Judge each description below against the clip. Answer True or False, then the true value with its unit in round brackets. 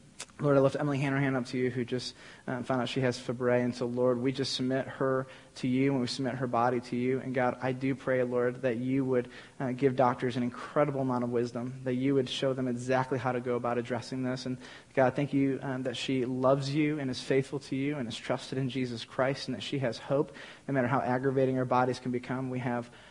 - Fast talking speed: True (255 wpm)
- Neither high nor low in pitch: False (130 Hz)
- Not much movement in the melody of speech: True (1.4 semitones)